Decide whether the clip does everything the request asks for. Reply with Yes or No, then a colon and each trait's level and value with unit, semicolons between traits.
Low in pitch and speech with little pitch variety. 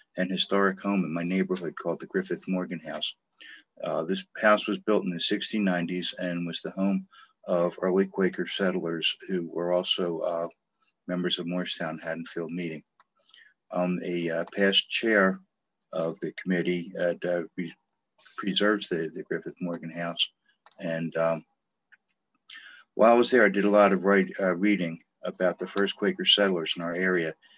Yes: very low, 90 Hz; narrow, 2.1 semitones